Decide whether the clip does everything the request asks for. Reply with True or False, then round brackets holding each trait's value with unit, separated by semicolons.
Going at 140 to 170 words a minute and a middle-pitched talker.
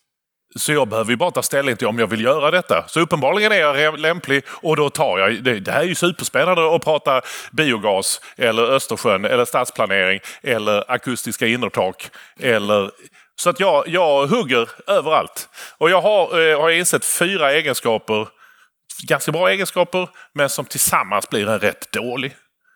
True (165 wpm; 150 Hz)